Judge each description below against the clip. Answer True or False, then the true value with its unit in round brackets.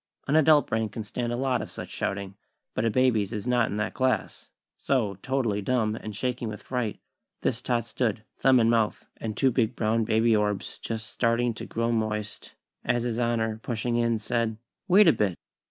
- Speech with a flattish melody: True (2.3 semitones)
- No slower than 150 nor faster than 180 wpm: False (200 wpm)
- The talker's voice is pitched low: True (115 Hz)